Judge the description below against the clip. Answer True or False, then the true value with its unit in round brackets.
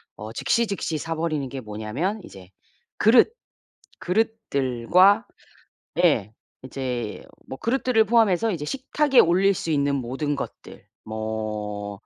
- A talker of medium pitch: True (150 Hz)